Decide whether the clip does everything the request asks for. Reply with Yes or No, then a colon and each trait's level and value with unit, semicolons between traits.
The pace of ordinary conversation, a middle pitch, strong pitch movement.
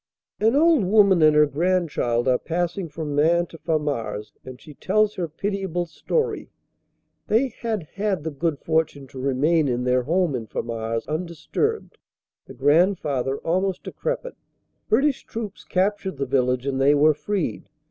Yes: average, 150 wpm; medium, 160 Hz; wide, 5.8 semitones